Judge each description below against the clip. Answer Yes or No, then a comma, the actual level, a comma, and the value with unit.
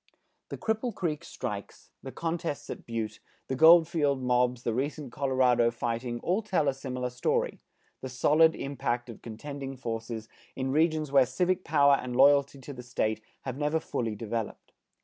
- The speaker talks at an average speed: Yes, average, 160 wpm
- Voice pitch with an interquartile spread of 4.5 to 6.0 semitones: No, average, 3.9 semitones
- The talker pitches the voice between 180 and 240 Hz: No, low, 135 Hz